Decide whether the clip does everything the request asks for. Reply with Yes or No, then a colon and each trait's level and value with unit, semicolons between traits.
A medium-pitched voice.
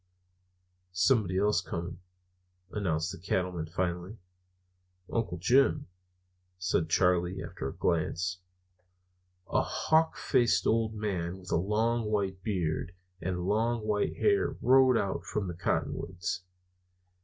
No: very low, 95 Hz